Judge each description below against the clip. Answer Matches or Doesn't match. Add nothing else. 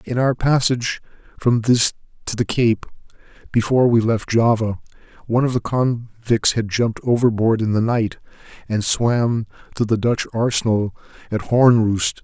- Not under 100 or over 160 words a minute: Matches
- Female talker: Doesn't match